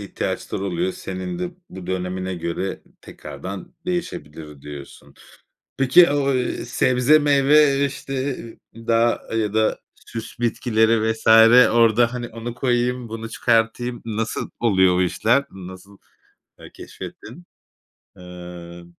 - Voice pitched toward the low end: Yes, low, 115 Hz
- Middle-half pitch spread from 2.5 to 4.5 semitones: No, average, 5.1 semitones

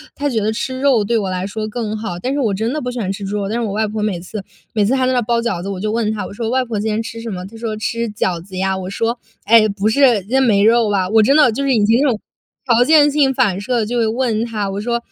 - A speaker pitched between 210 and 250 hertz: Yes, high, 220 Hz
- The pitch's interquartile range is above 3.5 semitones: No, average, 3.0 semitones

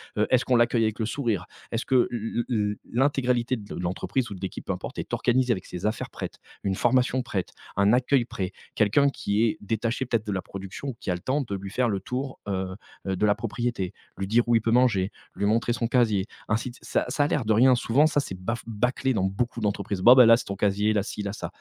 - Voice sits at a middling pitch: No, low, 115 Hz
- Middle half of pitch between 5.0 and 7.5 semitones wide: No, average, 3.6 semitones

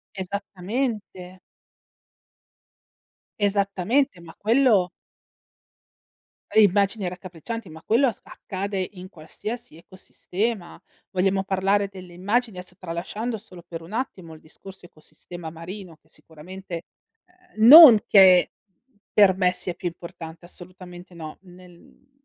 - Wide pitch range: No, average, 2.7 semitones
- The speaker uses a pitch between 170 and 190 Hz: Yes, medium, 185 Hz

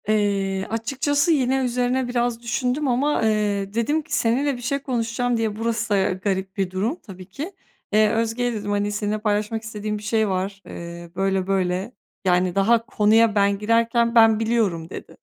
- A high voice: Yes, high, 220 Hz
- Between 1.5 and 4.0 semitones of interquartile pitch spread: Yes, average, 3.2 semitones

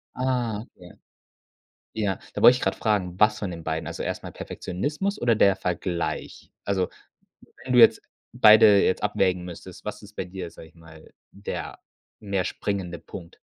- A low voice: Yes, low, 100 Hz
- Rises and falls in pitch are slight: No, average, 3.4 semitones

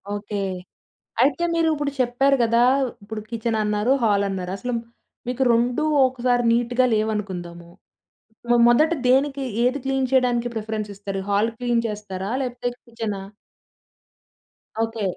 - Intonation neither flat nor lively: Yes, average, 3.3 semitones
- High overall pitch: Yes, high, 235 Hz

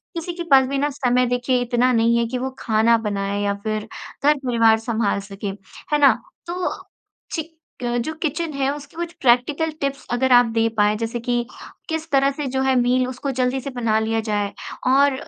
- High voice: Yes, very high, 250 Hz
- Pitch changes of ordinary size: Yes, average, 3.4 semitones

